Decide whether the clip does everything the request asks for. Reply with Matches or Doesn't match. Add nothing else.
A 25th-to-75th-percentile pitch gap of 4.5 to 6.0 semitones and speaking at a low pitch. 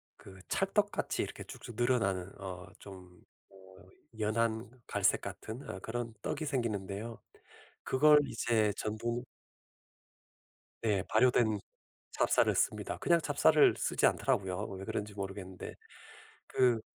Doesn't match